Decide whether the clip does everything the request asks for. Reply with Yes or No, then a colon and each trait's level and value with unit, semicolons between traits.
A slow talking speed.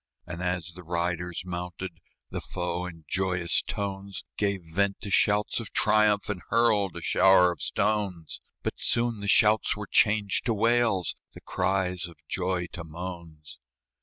No: average, 155 wpm